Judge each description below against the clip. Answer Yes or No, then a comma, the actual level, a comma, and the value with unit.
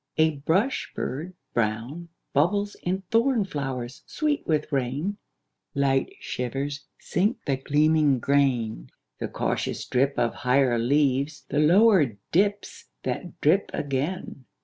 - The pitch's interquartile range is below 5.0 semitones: No, wide, 5.4 semitones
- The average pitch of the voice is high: No, medium, 145 Hz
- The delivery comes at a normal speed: No, slow, 120 wpm